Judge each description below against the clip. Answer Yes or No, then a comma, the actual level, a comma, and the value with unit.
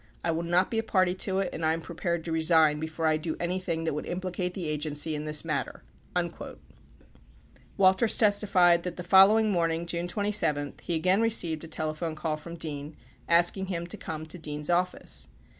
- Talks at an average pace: Yes, average, 195 wpm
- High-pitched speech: No, medium, 170 Hz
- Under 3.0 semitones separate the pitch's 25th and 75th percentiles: Yes, narrow, 2.6 semitones